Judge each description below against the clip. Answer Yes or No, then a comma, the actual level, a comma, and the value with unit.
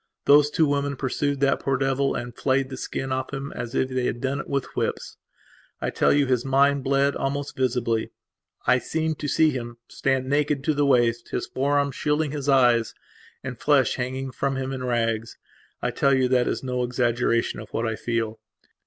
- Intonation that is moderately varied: No, narrow, 2.3 semitones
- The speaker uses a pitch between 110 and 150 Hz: Yes, low, 135 Hz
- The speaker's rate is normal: Yes, average, 195 wpm